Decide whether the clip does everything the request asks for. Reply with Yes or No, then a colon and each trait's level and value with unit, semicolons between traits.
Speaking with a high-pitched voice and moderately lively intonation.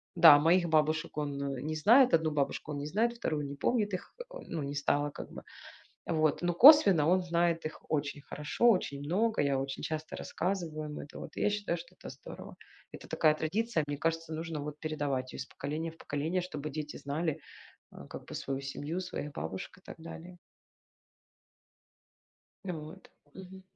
No: medium, 155 Hz; average, 3.4 semitones